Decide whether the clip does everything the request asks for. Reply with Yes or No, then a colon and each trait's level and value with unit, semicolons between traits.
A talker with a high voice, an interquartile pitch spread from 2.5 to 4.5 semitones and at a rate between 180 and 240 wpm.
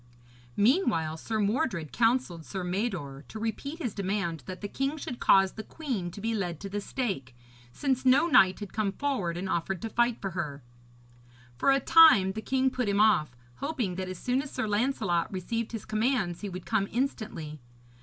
No: high, 205 Hz; wide, 5.5 semitones; average, 190 wpm